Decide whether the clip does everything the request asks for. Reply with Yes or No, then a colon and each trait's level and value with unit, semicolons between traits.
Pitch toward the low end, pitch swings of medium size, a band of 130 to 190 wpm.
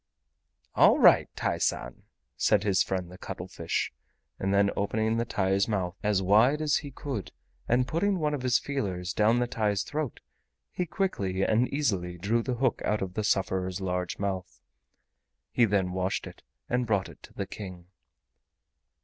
Yes: low, 100 Hz; average, 4.6 semitones; average, 165 wpm